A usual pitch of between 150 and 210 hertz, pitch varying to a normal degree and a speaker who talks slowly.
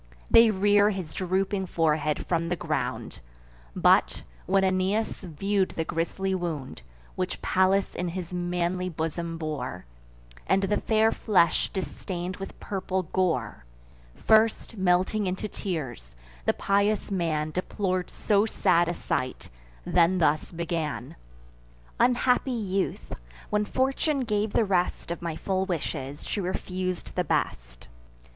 Yes: medium, 185 Hz; average, 3.1 semitones; slow, 125 wpm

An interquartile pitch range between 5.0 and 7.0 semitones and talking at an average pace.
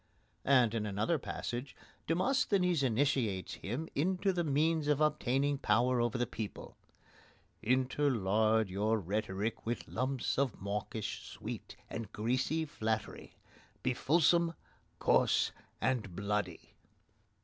No: wide, 5.4 semitones; slow, 110 wpm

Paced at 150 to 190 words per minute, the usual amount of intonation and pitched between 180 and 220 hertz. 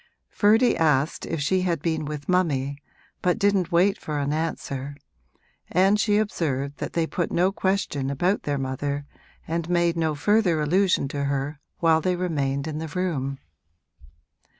No: average, 155 wpm; average, 4.3 semitones; medium, 160 Hz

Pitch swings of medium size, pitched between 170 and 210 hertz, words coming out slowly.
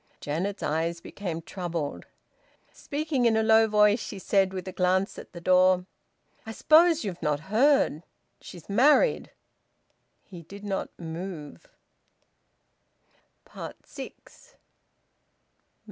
Yes: average, 4.5 semitones; high, 190 Hz; slow, 110 wpm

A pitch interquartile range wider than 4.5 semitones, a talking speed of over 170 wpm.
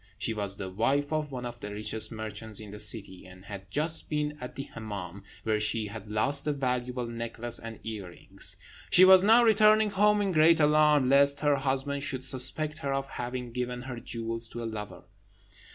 Yes: average, 5.2 semitones; average, 195 wpm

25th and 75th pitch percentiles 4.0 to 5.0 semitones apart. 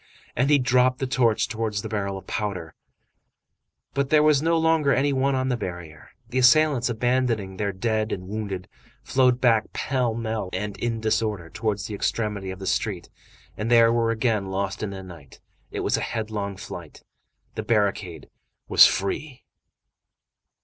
Yes: average, 4.3 semitones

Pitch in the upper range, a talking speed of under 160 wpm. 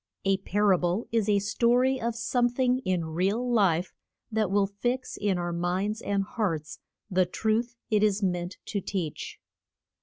No: high, 200 Hz; average, 175 wpm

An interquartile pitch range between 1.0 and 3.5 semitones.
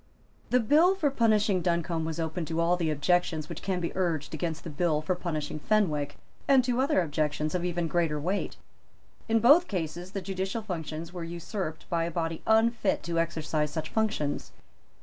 No: average, 4.2 semitones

